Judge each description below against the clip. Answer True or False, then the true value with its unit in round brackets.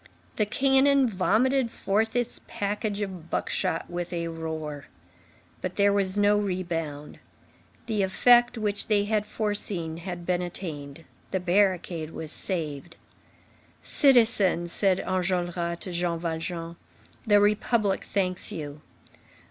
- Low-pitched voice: False (185 Hz)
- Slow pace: True (120 wpm)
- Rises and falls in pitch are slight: False (3.6 semitones)